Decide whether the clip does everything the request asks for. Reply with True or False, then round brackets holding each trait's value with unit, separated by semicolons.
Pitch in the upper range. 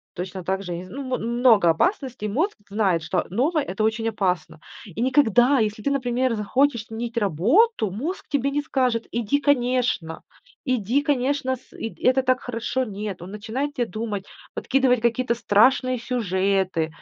True (235 Hz)